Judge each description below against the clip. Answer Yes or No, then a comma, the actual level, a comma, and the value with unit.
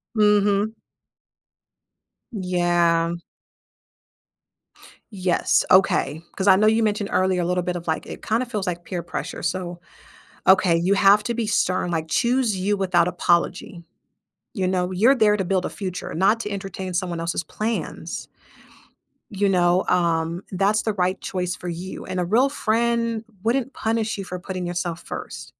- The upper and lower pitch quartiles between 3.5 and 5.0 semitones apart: No, average, 3.1 semitones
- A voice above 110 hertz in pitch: Yes, medium, 185 Hz